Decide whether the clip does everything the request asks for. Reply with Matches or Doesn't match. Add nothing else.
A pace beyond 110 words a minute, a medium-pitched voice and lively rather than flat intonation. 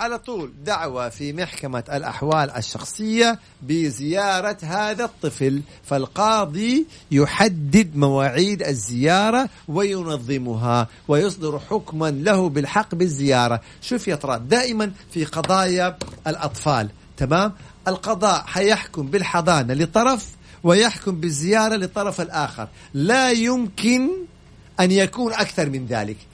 Doesn't match